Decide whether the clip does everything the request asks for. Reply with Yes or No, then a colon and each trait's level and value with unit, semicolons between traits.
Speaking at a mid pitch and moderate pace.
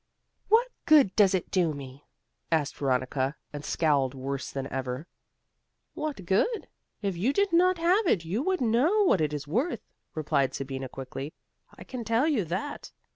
Yes: medium, 175 Hz; average, 165 wpm